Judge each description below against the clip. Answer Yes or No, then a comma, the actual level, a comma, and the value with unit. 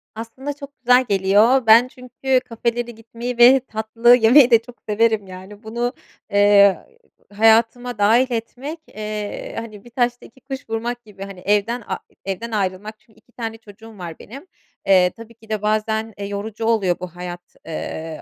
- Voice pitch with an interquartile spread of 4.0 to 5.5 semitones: No, average, 2.9 semitones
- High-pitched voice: Yes, high, 225 Hz